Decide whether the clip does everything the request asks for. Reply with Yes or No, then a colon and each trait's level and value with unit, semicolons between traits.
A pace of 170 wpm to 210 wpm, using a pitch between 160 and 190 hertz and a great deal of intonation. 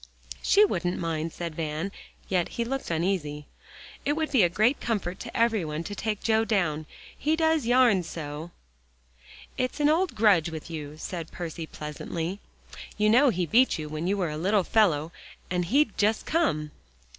Yes: average, 175 wpm; medium, 185 Hz; wide, 6.2 semitones